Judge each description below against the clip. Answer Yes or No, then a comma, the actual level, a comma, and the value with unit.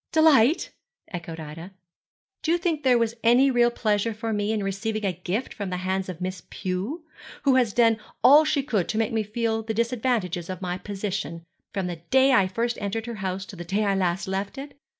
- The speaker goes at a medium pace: No, fast, 215 wpm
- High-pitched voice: Yes, high, 210 Hz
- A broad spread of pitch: No, average, 4.2 semitones